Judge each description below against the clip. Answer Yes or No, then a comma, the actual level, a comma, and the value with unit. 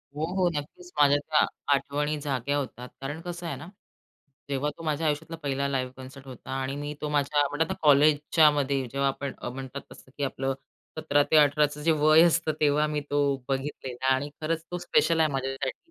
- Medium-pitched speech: Yes, medium, 145 Hz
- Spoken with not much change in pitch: Yes, narrow, 2.1 semitones